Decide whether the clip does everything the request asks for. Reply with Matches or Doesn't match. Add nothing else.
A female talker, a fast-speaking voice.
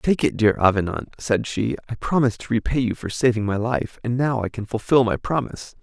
Doesn't match